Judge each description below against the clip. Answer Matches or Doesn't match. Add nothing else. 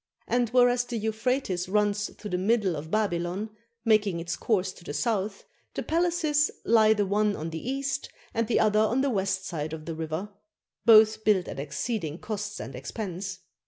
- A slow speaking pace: Doesn't match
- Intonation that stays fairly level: Doesn't match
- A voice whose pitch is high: Matches